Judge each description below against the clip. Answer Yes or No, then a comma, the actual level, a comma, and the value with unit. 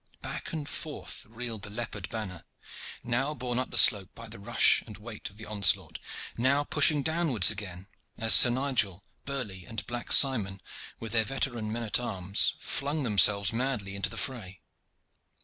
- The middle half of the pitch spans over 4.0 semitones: Yes, average, 4.4 semitones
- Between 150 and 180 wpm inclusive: Yes, average, 165 wpm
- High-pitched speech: No, low, 115 Hz